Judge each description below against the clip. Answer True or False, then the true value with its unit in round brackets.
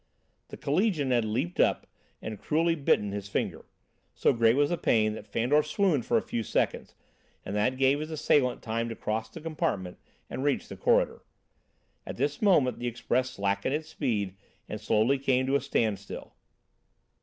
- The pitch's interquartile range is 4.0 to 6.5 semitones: True (5.1 semitones)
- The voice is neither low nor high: False (130 Hz)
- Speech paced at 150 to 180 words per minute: True (175 wpm)